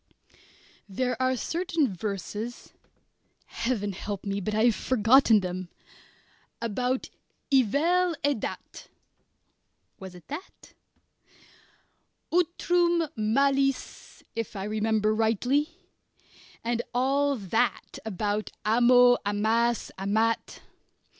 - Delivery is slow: Yes, slow, 95 wpm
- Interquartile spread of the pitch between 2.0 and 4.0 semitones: No, average, 4.5 semitones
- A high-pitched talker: Yes, high, 230 Hz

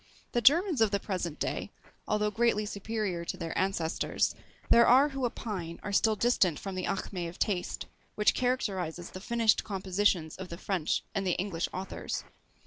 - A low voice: No, high, 200 Hz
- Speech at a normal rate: Yes, average, 170 wpm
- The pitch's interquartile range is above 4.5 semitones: No, average, 3.9 semitones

